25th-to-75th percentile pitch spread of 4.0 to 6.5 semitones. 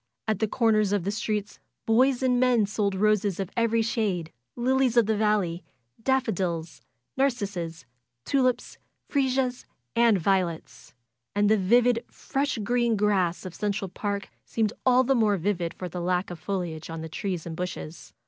Yes: average, 4.7 semitones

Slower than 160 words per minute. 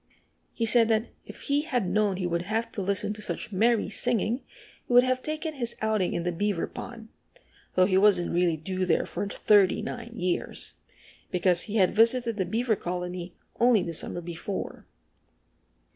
No: average, 175 wpm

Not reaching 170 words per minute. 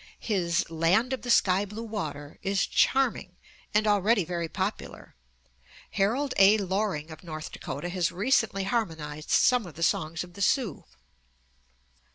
Yes: average, 145 wpm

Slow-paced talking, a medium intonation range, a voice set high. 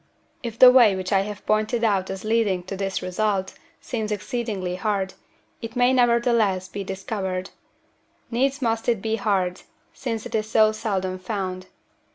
No: average, 160 wpm; average, 3.3 semitones; high, 210 Hz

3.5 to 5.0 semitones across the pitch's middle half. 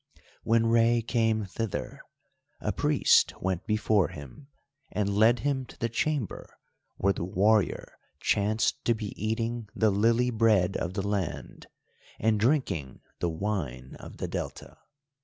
No: average, 2.9 semitones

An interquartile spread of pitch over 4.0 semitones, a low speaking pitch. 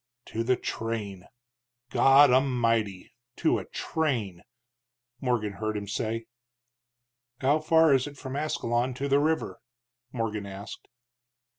Yes: average, 4.5 semitones; low, 120 Hz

